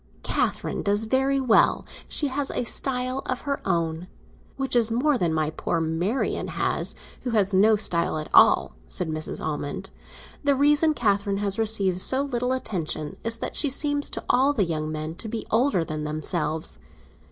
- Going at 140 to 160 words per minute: No, average, 170 wpm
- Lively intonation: Yes, wide, 8.0 semitones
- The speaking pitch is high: Yes, high, 215 Hz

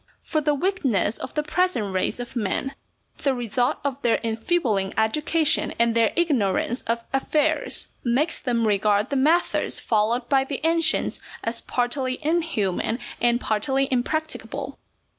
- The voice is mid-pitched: No, very high, 250 Hz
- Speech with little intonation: No, average, 5.0 semitones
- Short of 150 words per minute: Yes, average, 140 wpm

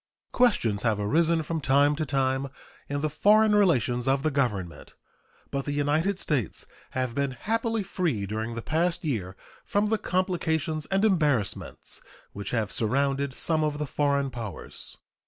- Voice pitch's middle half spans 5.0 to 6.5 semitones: Yes, wide, 5.4 semitones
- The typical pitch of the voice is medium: Yes, medium, 145 Hz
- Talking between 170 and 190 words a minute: No, average, 155 wpm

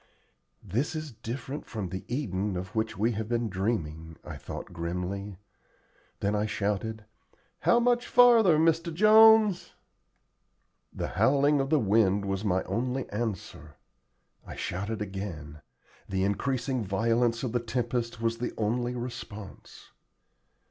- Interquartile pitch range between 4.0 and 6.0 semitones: Yes, average, 5.1 semitones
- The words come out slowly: Yes, slow, 130 wpm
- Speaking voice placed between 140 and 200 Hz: No, low, 115 Hz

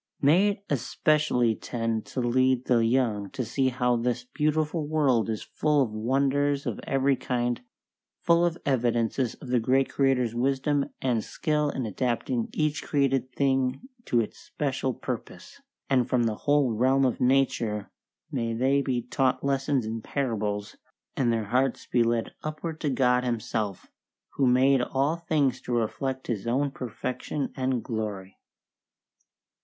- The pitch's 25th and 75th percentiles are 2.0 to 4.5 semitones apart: Yes, average, 2.9 semitones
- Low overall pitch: Yes, low, 130 Hz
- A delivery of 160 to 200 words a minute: No, average, 150 wpm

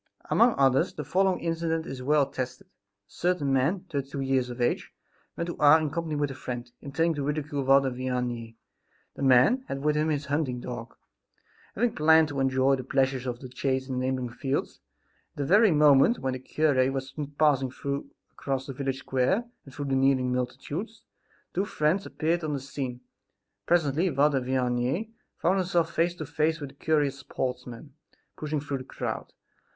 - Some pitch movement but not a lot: Yes, average, 3.3 semitones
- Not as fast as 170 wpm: No, average, 185 wpm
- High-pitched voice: No, medium, 140 Hz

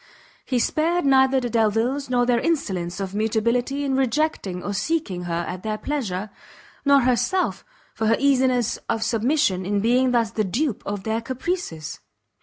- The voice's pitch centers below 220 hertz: No, high, 235 Hz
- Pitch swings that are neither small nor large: Yes, average, 4.7 semitones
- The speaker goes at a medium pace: Yes, average, 160 wpm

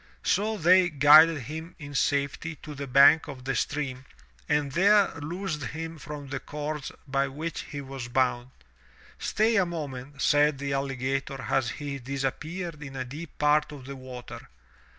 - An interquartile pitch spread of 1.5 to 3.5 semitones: Yes, average, 2.8 semitones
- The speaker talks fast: No, average, 160 wpm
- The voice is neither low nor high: Yes, medium, 145 Hz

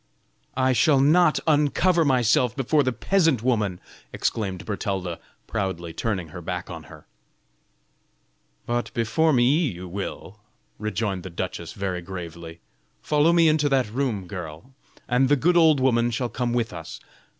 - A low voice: Yes, low, 120 Hz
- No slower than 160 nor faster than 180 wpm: No, average, 145 wpm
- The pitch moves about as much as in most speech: No, wide, 7.0 semitones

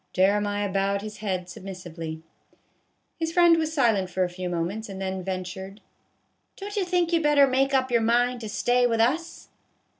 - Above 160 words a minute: Yes, average, 185 wpm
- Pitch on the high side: Yes, high, 210 Hz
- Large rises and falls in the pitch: Yes, wide, 6.3 semitones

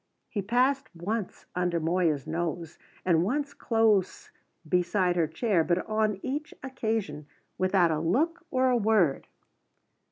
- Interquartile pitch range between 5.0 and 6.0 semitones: Yes, wide, 5.6 semitones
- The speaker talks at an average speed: No, slow, 130 wpm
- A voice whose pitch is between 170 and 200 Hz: Yes, high, 190 Hz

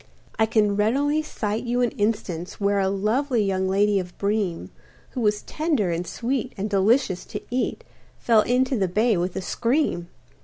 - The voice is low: No, high, 210 Hz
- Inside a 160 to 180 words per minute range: Yes, average, 170 wpm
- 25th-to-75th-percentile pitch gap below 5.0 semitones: Yes, average, 4.1 semitones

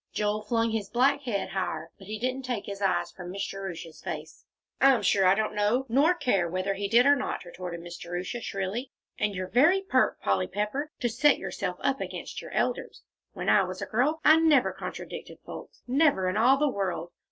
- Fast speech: Yes, fast, 210 wpm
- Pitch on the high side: Yes, high, 210 Hz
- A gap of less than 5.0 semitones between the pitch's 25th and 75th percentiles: No, wide, 5.6 semitones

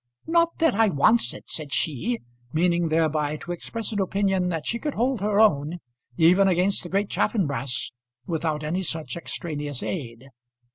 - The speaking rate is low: No, average, 160 wpm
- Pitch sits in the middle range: Yes, medium, 175 Hz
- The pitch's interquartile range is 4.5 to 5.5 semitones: Yes, average, 4.9 semitones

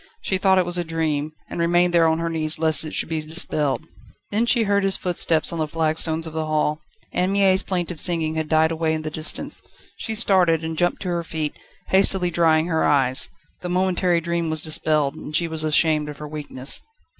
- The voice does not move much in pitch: Yes, narrow, 2.2 semitones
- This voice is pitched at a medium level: Yes, medium, 160 Hz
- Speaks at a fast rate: Yes, fast, 215 wpm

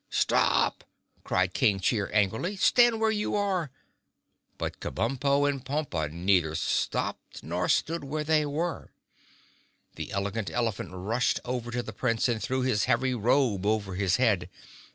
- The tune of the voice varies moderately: No, wide, 6.4 semitones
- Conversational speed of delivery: Yes, average, 145 wpm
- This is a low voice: Yes, low, 120 Hz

